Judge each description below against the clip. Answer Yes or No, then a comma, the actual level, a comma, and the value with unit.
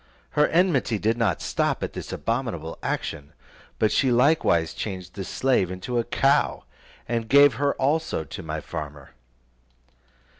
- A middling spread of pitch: No, wide, 7.4 semitones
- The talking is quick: No, average, 145 wpm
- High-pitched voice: No, low, 115 Hz